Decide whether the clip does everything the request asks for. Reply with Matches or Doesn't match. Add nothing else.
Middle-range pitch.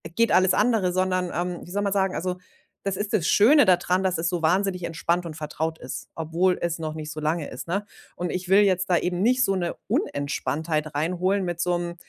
Matches